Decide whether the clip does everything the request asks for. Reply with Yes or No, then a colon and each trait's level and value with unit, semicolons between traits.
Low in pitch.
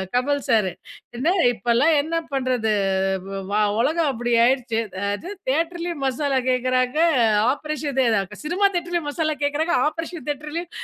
No: very high, 285 Hz